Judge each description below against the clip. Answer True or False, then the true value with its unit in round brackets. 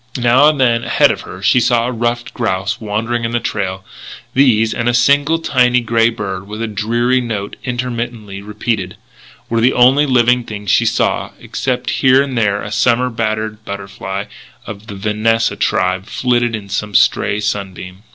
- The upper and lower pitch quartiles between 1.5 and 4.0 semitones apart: True (3.1 semitones)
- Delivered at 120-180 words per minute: True (170 wpm)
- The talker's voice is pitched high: False (115 Hz)